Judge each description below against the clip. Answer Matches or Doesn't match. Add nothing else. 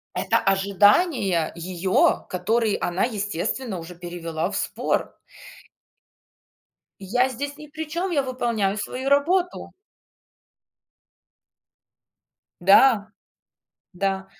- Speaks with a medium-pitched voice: Doesn't match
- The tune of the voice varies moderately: Doesn't match